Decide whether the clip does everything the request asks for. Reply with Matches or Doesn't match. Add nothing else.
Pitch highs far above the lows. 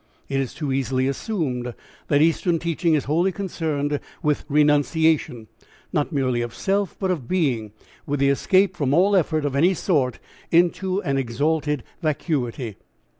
Doesn't match